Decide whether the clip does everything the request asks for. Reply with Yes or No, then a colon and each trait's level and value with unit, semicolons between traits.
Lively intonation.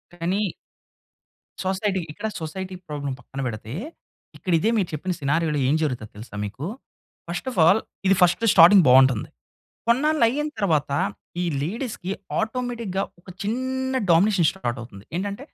Yes: wide, 6.6 semitones